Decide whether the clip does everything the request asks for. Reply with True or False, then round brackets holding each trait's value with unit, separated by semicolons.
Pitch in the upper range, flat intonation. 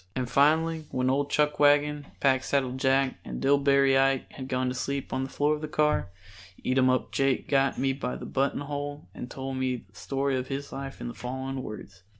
False (135 Hz; 1.6 semitones)